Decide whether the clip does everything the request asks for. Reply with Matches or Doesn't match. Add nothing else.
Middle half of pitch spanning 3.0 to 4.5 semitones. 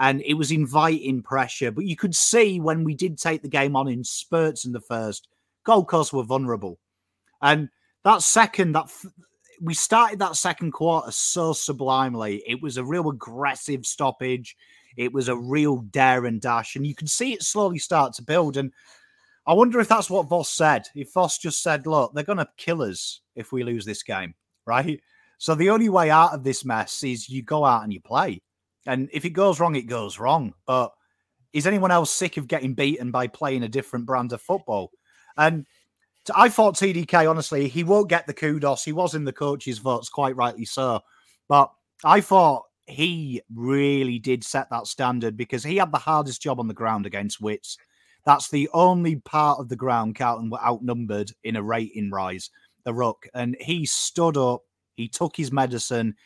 Doesn't match